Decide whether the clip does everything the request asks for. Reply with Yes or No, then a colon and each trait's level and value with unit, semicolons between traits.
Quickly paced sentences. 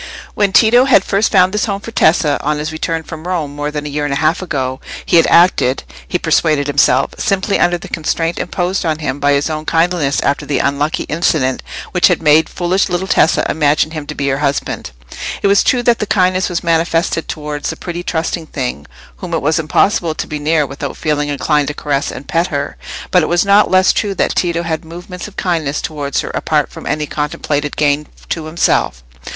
Yes: fast, 215 wpm